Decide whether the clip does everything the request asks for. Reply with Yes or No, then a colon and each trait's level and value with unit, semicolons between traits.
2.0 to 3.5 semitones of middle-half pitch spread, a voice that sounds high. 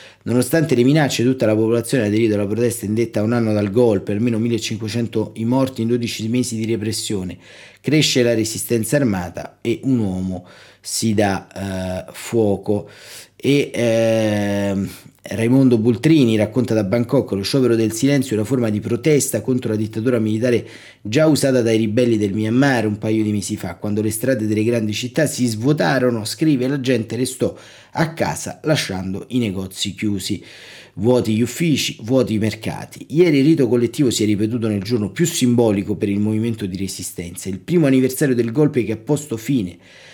No: average, 3.1 semitones; low, 115 Hz